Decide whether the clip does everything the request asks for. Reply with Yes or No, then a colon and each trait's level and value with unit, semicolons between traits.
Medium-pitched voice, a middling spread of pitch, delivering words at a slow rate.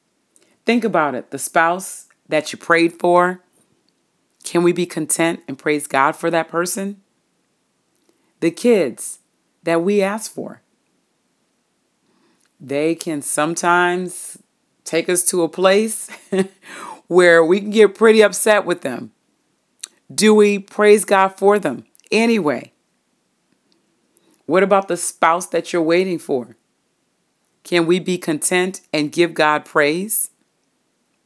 Yes: medium, 175 Hz; average, 3.0 semitones; slow, 125 wpm